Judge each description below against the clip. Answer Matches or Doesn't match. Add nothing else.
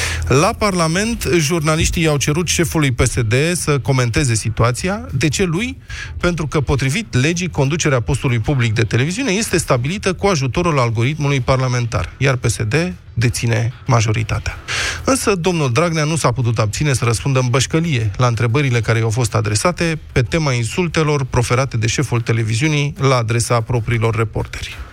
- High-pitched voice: Doesn't match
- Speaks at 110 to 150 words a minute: Matches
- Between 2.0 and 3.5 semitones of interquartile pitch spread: Doesn't match